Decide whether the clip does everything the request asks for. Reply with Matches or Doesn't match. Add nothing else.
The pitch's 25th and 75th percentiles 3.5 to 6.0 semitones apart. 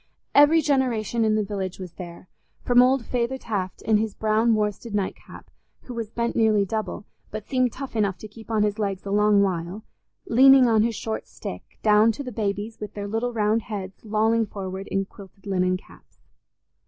Doesn't match